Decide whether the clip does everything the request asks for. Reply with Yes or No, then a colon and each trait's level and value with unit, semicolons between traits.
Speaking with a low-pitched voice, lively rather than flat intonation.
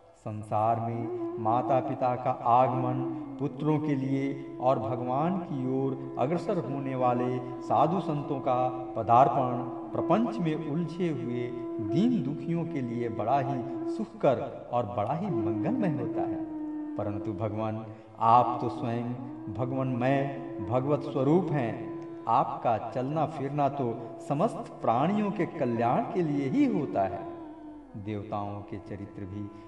Yes: low, 130 Hz; wide, 7.1 semitones